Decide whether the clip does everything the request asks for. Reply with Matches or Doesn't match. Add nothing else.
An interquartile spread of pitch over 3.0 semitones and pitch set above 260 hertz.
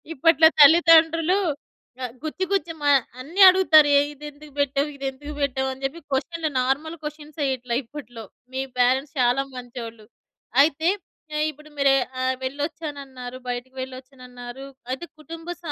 Matches